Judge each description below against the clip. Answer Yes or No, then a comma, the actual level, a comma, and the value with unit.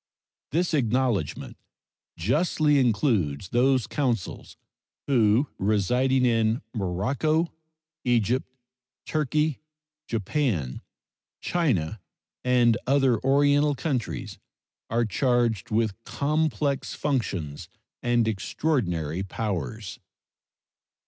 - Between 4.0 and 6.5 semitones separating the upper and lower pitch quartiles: Yes, average, 5.2 semitones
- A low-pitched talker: Yes, low, 120 Hz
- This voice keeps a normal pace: No, slow, 75 wpm